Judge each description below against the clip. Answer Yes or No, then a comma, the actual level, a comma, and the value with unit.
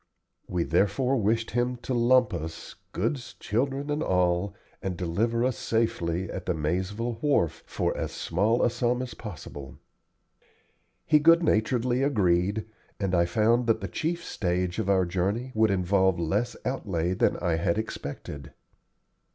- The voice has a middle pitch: No, low, 105 Hz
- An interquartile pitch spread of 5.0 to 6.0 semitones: Yes, wide, 5.5 semitones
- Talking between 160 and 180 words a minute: No, average, 150 wpm